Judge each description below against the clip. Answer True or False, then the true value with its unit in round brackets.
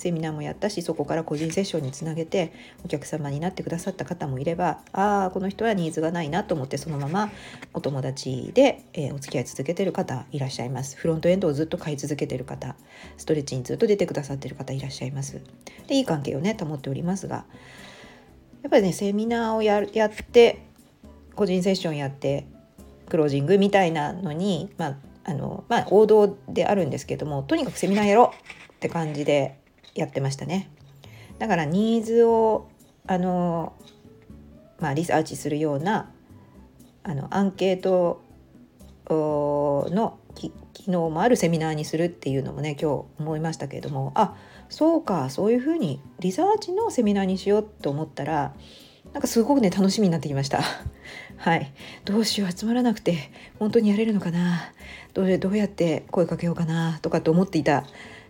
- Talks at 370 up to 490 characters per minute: True (390 characters per minute)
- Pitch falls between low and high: True (165 Hz)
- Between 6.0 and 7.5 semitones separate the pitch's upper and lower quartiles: False (5.3 semitones)